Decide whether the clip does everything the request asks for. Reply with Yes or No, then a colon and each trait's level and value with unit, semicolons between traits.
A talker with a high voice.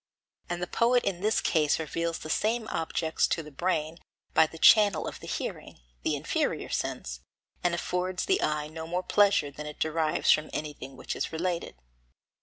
No: medium, 165 Hz